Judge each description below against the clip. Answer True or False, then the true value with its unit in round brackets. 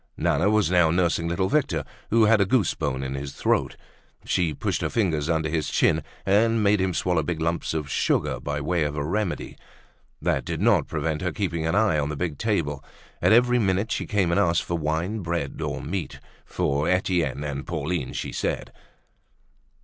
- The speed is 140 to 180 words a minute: False (195 wpm)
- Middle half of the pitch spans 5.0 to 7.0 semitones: False (4.5 semitones)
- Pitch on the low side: True (85 Hz)